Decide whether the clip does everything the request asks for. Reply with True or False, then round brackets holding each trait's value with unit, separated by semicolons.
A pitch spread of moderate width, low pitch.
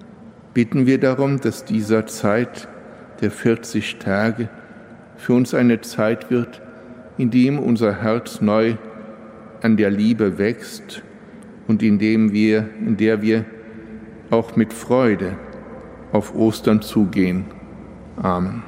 False (1.4 semitones; 110 Hz)